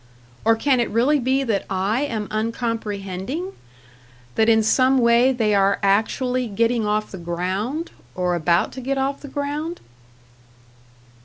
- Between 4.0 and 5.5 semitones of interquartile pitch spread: Yes, average, 4.7 semitones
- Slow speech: No, average, 145 wpm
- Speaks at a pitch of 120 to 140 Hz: No, high, 230 Hz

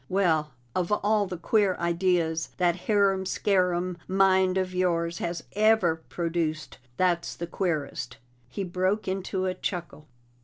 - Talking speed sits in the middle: No, slow, 130 wpm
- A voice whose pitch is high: No, medium, 180 Hz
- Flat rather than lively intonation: Yes, narrow, 2.1 semitones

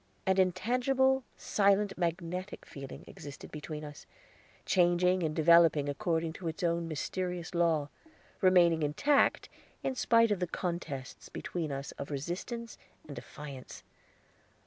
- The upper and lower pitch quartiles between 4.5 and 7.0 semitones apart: No, average, 3.6 semitones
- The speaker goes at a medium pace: No, slow, 125 wpm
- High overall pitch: No, medium, 170 Hz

